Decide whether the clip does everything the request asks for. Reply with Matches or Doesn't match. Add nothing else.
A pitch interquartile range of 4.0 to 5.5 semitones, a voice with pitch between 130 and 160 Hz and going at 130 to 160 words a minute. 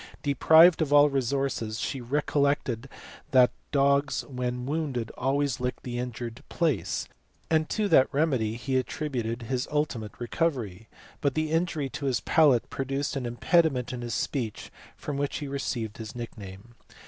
Doesn't match